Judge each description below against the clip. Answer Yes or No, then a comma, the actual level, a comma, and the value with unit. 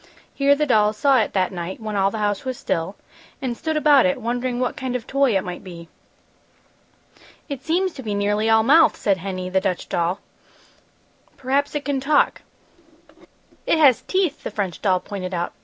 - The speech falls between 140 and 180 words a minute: No, average, 190 wpm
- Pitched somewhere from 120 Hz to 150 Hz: No, high, 225 Hz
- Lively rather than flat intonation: Yes, wide, 6.3 semitones